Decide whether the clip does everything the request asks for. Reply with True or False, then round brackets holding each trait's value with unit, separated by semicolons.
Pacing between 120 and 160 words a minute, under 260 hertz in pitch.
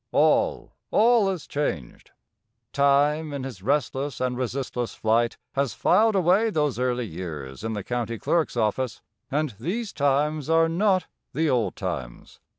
True (145 wpm; 140 Hz)